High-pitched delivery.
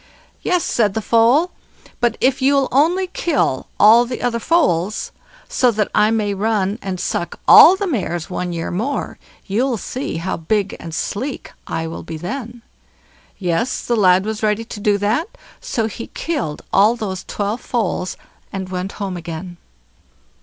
Yes: high, 215 Hz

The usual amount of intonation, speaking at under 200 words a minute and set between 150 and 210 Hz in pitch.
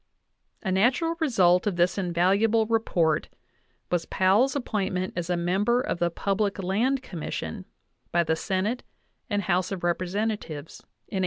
Yes: average, 3.8 semitones; average, 145 wpm; high, 190 Hz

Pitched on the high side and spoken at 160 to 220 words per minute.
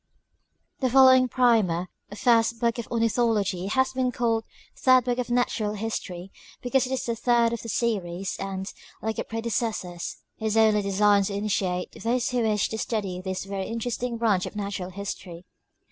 Yes: high, 220 Hz; average, 170 wpm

